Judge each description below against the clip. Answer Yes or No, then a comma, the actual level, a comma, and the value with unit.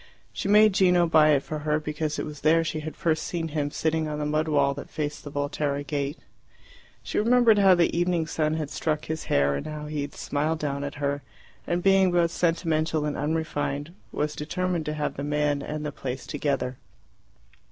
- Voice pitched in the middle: Yes, medium, 155 Hz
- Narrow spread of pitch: Yes, narrow, 2.1 semitones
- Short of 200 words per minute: No, fast, 205 wpm